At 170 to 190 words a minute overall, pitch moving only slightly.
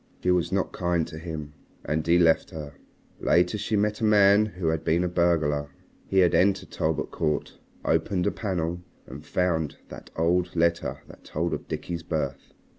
Yes: average, 180 wpm; narrow, 2.2 semitones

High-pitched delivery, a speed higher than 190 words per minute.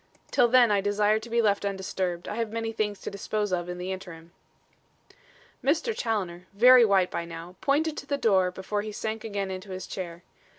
Yes: high, 205 Hz; average, 200 wpm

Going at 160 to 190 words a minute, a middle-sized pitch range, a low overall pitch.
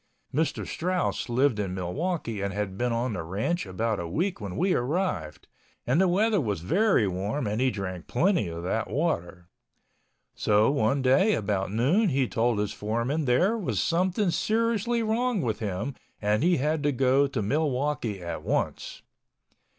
No: average, 165 wpm; wide, 8.9 semitones; low, 130 Hz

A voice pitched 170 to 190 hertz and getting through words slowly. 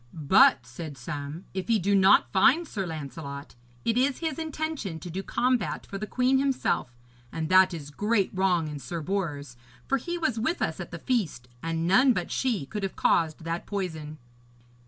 No: medium, 185 Hz; average, 185 wpm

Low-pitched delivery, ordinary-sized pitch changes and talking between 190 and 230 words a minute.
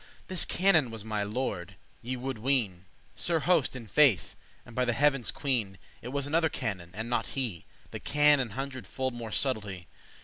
Yes: low, 125 Hz; average, 4.3 semitones; average, 195 wpm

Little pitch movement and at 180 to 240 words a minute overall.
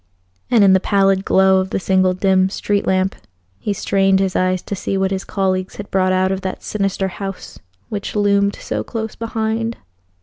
Yes: narrow, 1.2 semitones; average, 190 wpm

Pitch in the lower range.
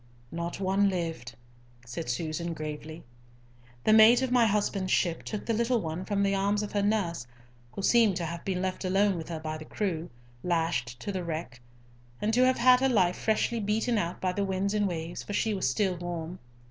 No: medium, 185 Hz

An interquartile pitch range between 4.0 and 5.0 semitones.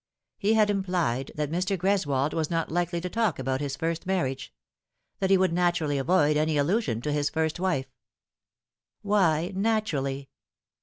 Yes: average, 4.7 semitones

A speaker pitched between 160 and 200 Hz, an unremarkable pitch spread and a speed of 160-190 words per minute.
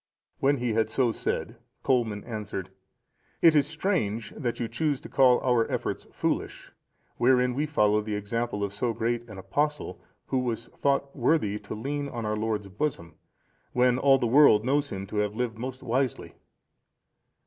No: low, 120 Hz; average, 4.3 semitones; average, 170 wpm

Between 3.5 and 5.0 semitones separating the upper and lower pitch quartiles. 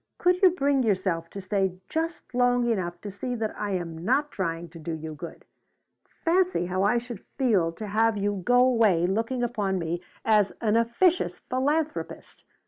No: wide, 5.4 semitones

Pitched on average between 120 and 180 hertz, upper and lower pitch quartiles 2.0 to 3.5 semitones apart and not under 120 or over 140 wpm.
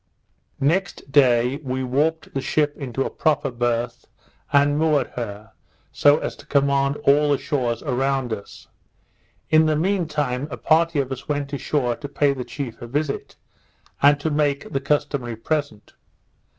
No: medium, 140 Hz; average, 2.8 semitones; average, 160 wpm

